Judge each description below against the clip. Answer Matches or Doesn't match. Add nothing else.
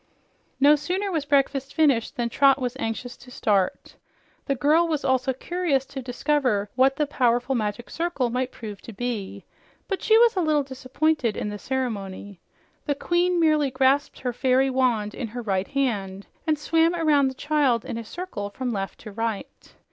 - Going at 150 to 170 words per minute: Doesn't match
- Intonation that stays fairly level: Doesn't match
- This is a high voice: Matches